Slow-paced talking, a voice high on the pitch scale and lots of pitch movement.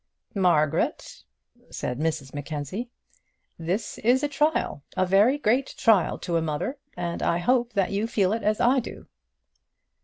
No: average, 150 wpm; high, 200 Hz; wide, 6.7 semitones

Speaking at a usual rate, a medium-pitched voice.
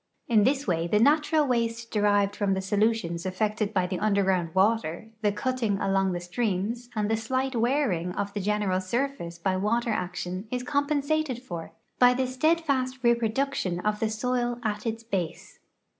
No: average, 170 wpm; high, 220 Hz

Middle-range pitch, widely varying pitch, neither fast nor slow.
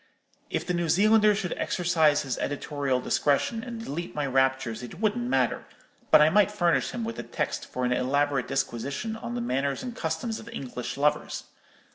Yes: medium, 160 Hz; wide, 7.9 semitones; average, 180 wpm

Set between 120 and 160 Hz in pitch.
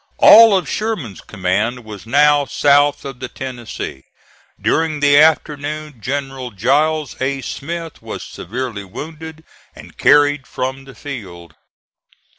Yes: medium, 140 Hz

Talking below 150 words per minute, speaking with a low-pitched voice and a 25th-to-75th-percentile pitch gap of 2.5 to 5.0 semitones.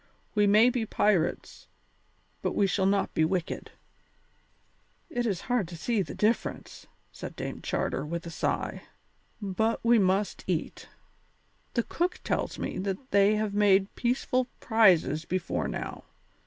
No: average, 140 wpm; high, 200 Hz; average, 3.5 semitones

